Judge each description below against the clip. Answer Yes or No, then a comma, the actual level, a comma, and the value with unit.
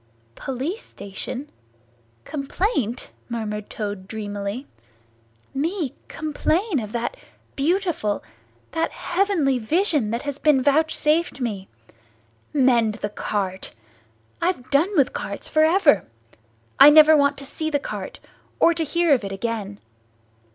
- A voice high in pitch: Yes, very high, 275 Hz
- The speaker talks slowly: Yes, slow, 120 wpm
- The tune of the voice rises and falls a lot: Yes, wide, 6.5 semitones